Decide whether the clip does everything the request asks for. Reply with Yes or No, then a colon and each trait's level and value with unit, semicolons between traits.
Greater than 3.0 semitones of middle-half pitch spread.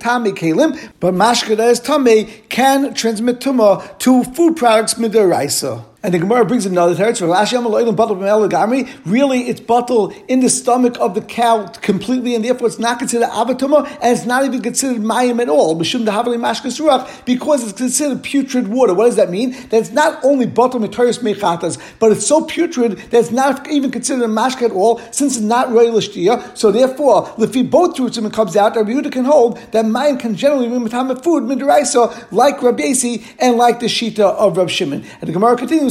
No: average, 2.7 semitones